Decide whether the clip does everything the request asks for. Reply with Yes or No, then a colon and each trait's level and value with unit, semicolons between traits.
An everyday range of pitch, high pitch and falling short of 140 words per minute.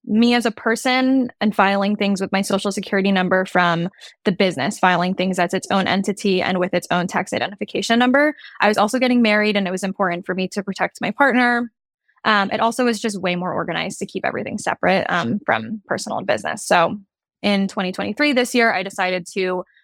No: average, 3.6 semitones; high, 200 Hz; fast, 205 wpm